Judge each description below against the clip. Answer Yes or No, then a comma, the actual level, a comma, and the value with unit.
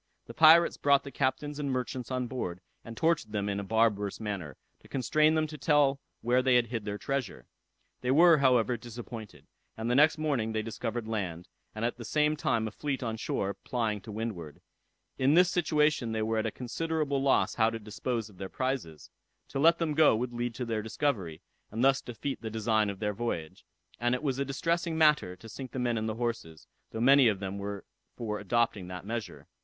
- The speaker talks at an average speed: No, fast, 210 wpm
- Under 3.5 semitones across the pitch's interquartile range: No, average, 4.4 semitones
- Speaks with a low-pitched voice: Yes, low, 120 Hz